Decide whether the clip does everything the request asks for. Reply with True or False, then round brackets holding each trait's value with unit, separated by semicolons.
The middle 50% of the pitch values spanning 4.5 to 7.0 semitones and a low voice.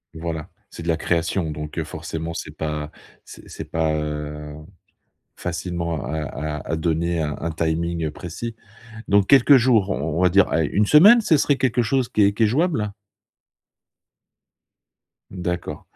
True (4.9 semitones; 85 Hz)